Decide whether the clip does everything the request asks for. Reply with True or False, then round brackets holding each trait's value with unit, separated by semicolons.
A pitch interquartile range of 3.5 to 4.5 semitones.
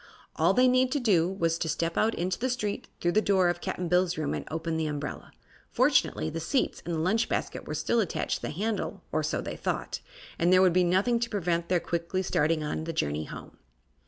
True (3.9 semitones)